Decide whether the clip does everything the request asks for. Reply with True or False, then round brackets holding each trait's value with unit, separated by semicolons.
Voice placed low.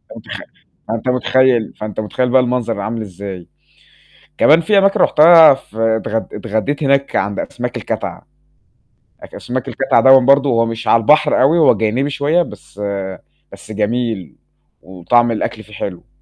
True (120 Hz)